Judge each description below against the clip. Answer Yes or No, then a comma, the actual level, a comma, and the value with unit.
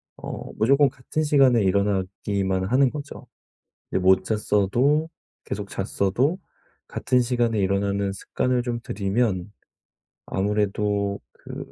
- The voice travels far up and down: No, average, 4.4 semitones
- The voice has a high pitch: No, low, 105 Hz